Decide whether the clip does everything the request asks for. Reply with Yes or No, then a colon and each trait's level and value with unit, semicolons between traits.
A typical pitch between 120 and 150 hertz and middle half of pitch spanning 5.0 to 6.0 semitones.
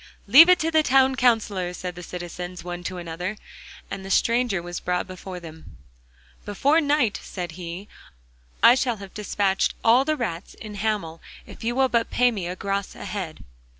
No: high, 200 Hz; wide, 5.4 semitones